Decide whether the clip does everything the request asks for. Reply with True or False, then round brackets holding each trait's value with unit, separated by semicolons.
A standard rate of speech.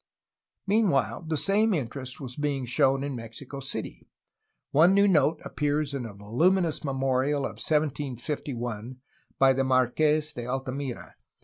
False (130 wpm)